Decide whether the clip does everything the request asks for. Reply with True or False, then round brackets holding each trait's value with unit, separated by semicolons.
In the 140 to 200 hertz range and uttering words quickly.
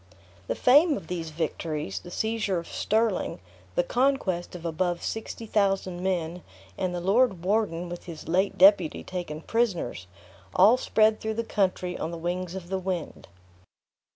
False (185 Hz; 155 wpm)